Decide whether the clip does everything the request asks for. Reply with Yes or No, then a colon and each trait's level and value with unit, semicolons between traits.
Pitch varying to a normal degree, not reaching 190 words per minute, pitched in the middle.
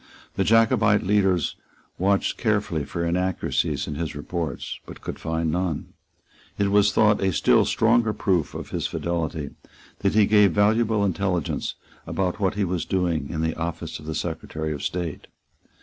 No: average, 4.1 semitones; average, 155 wpm; very low, 90 Hz